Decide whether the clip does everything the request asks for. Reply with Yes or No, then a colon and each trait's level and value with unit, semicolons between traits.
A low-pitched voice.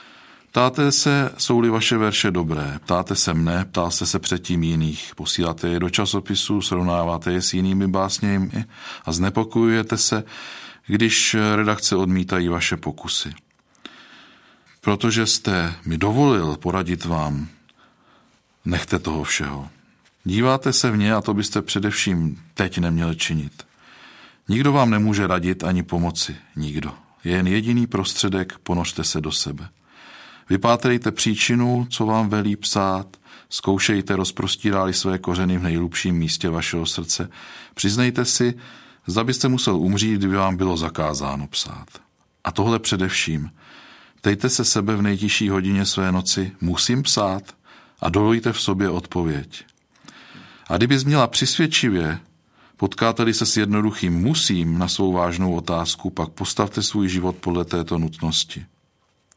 Yes: very low, 95 Hz